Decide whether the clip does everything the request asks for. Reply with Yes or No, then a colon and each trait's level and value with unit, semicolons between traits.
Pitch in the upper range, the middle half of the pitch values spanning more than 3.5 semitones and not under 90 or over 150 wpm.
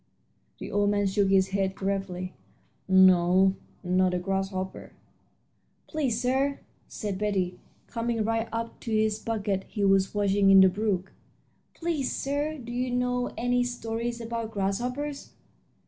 Yes: high, 210 Hz; average, 3.9 semitones; slow, 135 wpm